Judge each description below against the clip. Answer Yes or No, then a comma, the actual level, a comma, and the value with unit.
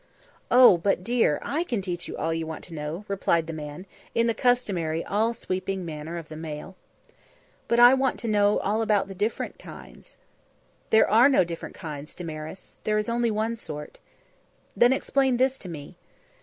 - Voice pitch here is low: No, high, 195 Hz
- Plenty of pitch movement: Yes, wide, 6.1 semitones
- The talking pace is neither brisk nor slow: Yes, average, 185 wpm